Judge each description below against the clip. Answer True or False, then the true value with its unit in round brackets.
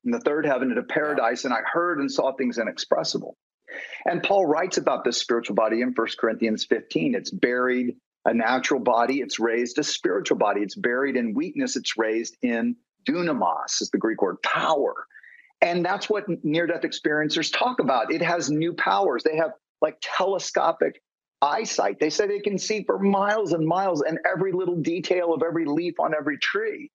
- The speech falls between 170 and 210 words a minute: True (185 wpm)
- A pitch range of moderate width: False (8.4 semitones)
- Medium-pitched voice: True (175 Hz)